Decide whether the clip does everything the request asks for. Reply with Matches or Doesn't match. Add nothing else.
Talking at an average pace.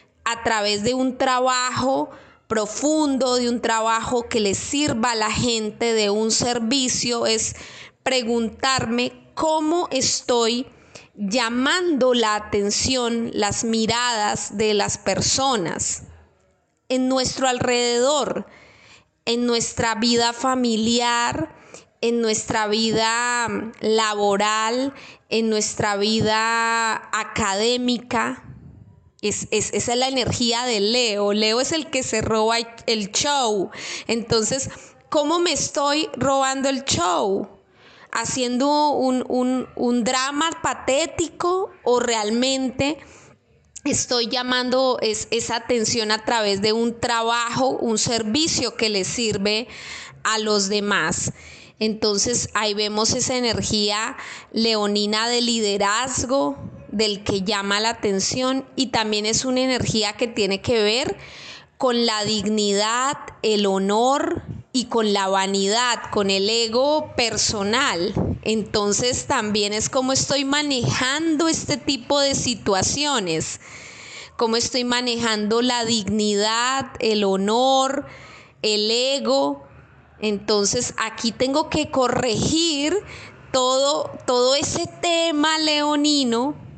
Doesn't match